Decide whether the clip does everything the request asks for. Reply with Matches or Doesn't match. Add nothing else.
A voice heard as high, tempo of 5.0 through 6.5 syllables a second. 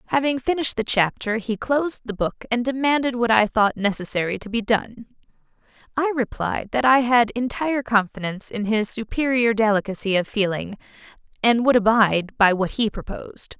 Matches